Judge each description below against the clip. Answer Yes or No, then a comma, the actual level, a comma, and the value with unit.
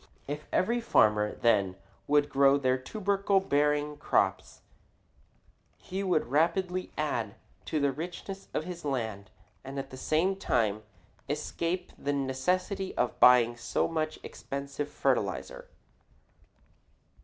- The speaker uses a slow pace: Yes, slow, 120 wpm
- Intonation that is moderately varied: No, wide, 5.8 semitones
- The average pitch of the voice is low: No, medium, 145 Hz